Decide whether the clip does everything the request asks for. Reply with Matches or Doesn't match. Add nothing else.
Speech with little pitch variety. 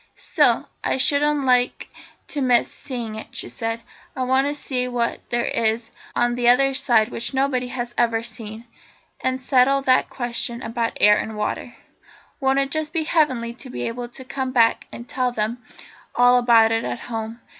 Matches